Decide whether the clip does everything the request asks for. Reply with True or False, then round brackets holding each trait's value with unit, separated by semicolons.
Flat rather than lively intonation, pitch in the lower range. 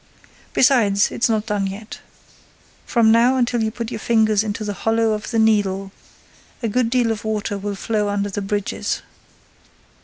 False (2.0 semitones; 220 Hz)